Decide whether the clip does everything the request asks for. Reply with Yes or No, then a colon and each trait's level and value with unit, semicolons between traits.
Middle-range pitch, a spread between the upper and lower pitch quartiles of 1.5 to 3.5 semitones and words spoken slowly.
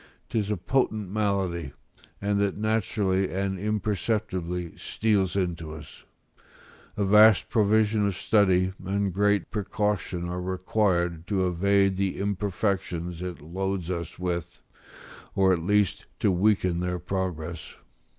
No: very low, 95 Hz; narrow, 2.5 semitones; slow, 120 wpm